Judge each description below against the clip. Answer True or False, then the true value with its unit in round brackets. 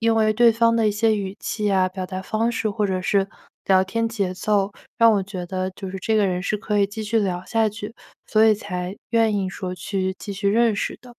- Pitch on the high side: True (205 Hz)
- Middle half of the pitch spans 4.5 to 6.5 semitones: False (2.7 semitones)